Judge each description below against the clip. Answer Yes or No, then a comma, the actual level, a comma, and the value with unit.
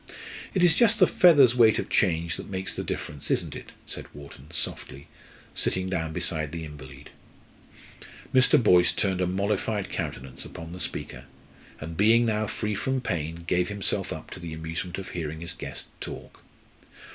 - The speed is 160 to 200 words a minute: Yes, average, 170 wpm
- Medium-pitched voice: No, very low, 90 Hz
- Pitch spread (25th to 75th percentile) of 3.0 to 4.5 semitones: No, average, 5.0 semitones